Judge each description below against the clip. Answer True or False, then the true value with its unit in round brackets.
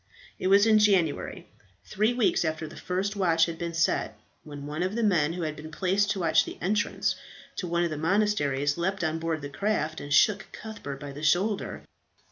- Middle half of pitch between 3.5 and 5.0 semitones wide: True (4.4 semitones)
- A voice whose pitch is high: False (170 Hz)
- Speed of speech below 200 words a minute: False (205 wpm)